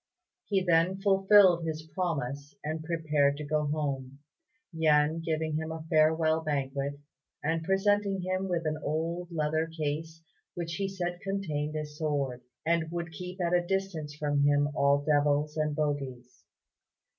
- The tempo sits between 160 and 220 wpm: No, average, 145 wpm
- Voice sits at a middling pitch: Yes, medium, 160 Hz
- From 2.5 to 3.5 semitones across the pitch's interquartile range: Yes, average, 2.8 semitones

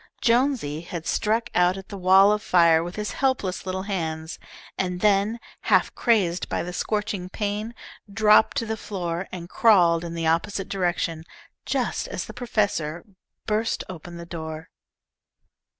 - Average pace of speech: Yes, average, 150 wpm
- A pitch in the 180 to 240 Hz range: Yes, medium, 185 Hz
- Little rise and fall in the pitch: No, average, 3.8 semitones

